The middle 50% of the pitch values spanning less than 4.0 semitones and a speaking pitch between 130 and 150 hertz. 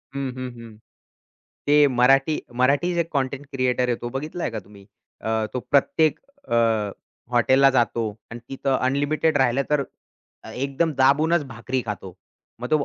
Yes: average, 2.9 semitones; low, 135 Hz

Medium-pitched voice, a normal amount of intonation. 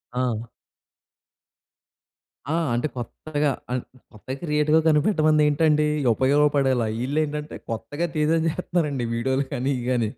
Yes: medium, 145 Hz; average, 3.2 semitones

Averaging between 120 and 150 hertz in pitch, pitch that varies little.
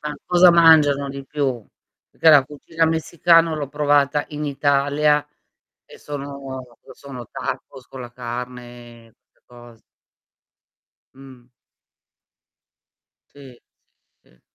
No: medium, 140 Hz; average, 3.1 semitones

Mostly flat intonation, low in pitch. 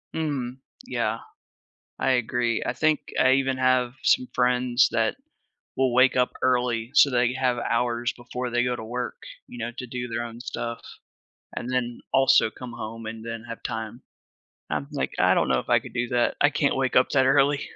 Yes: narrow, 1.6 semitones; low, 125 Hz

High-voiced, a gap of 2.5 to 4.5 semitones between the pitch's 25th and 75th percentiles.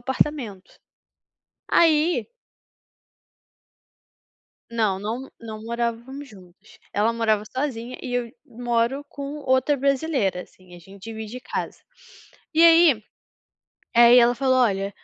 Yes: high, 235 Hz; average, 3.9 semitones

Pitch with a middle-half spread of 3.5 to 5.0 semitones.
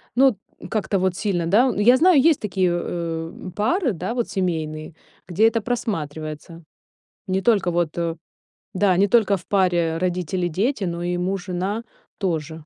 Yes: average, 3.9 semitones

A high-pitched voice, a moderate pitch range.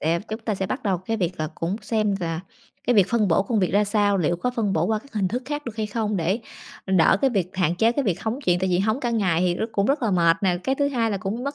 Yes: high, 205 Hz; average, 4.1 semitones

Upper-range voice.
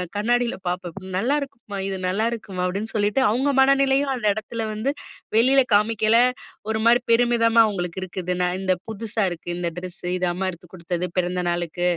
Yes: high, 205 Hz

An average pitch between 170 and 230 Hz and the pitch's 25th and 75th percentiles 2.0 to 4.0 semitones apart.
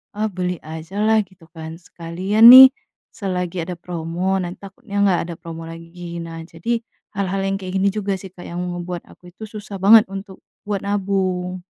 Yes: medium, 185 Hz; narrow, 2.5 semitones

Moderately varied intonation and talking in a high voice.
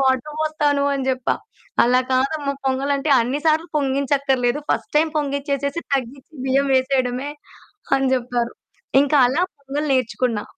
No: narrow, 1.9 semitones; very high, 275 Hz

